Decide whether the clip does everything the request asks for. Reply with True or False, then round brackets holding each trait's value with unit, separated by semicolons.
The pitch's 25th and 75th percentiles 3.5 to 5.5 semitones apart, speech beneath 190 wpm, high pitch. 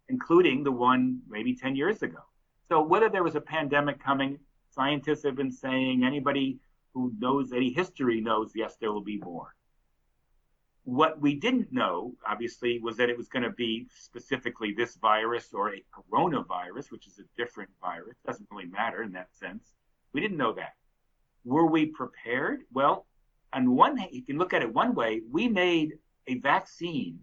False (4.6 semitones; 175 wpm; 135 Hz)